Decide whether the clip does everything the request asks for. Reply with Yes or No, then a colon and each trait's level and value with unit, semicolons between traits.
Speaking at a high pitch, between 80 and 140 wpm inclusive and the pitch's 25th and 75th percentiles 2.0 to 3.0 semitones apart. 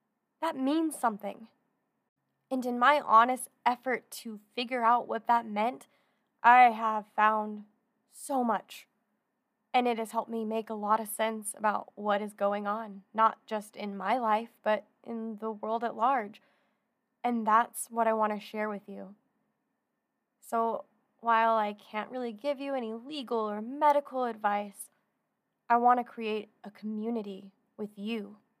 No: high, 225 Hz; average, 155 wpm; narrow, 2.5 semitones